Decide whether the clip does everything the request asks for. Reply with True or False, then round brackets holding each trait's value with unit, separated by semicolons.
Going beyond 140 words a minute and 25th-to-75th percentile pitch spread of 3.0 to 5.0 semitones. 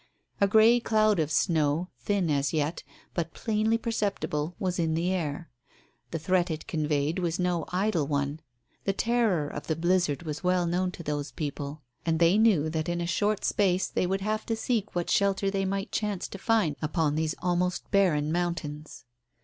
True (180 wpm; 4.1 semitones)